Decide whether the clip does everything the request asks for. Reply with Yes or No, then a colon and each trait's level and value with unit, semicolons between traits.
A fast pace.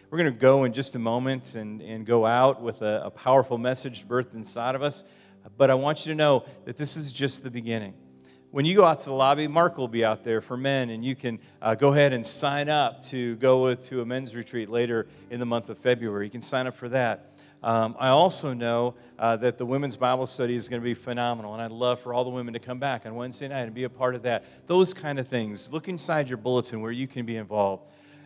Yes: fast, 255 wpm